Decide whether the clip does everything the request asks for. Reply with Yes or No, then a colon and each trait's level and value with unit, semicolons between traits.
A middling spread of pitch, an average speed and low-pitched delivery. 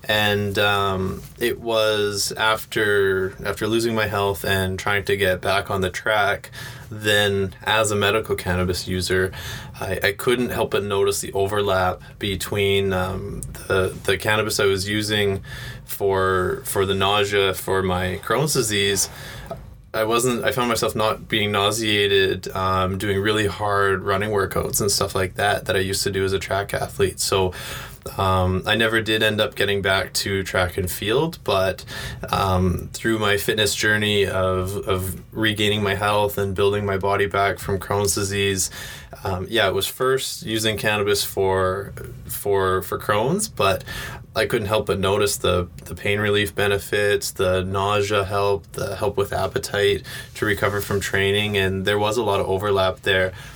No: narrow, 1.9 semitones; average, 165 wpm; low, 100 Hz